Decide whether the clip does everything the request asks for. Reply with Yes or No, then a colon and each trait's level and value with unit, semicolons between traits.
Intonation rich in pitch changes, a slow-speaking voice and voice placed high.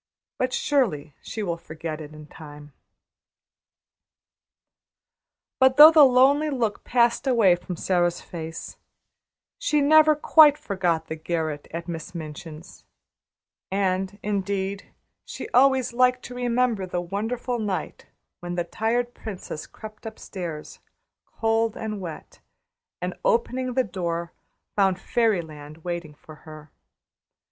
Yes: wide, 6.7 semitones; slow, 120 wpm; high, 195 Hz